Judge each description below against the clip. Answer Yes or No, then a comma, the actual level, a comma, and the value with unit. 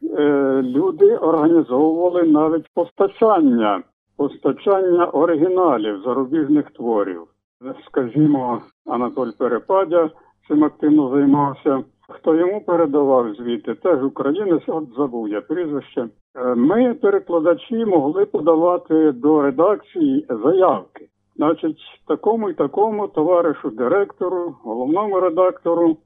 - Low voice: No, medium, 160 Hz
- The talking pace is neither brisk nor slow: No, slow, 90 wpm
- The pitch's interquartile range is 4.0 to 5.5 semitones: Yes, average, 4.7 semitones